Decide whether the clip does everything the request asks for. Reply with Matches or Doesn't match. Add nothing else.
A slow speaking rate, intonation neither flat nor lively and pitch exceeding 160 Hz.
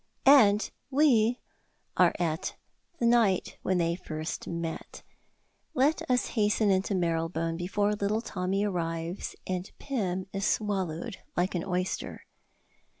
Matches